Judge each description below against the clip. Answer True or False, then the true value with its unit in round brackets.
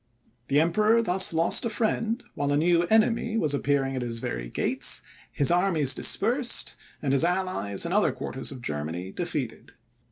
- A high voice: False (165 Hz)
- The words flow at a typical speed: True (165 wpm)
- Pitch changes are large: True (7.7 semitones)